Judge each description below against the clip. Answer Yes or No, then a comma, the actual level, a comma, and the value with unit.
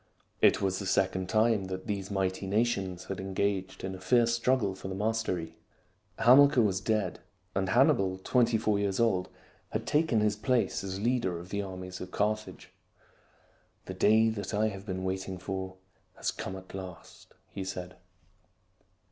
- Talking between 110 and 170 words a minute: Yes, average, 165 wpm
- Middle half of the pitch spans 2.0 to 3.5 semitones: Yes, average, 2.7 semitones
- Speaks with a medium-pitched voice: No, very low, 95 Hz